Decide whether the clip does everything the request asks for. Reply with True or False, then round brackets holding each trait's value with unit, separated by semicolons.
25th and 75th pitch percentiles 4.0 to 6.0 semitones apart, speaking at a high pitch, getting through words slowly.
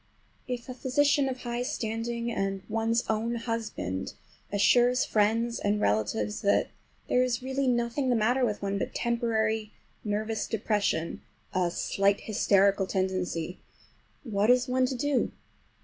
False (3.5 semitones; 225 Hz; 130 wpm)